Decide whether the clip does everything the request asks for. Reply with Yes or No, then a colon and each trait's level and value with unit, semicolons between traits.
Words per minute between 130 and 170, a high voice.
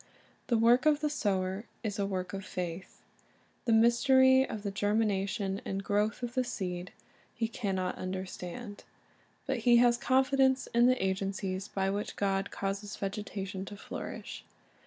Yes: average, 145 wpm; high, 205 Hz